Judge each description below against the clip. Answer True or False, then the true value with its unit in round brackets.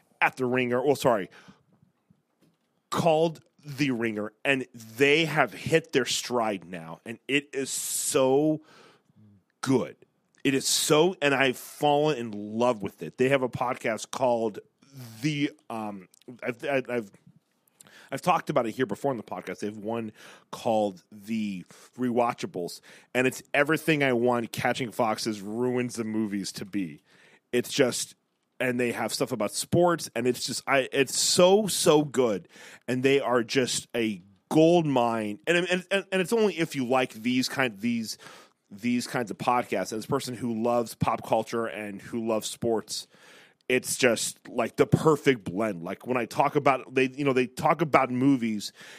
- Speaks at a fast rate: False (165 wpm)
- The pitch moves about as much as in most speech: True (4.2 semitones)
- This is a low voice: True (125 Hz)